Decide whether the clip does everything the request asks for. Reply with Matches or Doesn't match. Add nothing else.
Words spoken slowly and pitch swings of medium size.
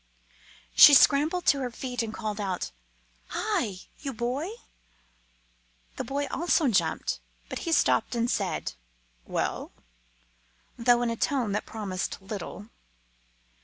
Matches